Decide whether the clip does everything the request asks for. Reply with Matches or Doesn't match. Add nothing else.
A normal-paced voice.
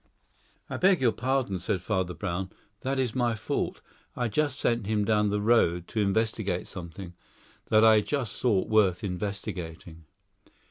Matches